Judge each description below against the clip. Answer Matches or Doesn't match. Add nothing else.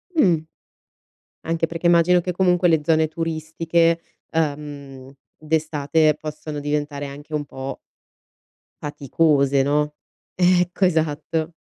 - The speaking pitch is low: Doesn't match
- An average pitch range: Doesn't match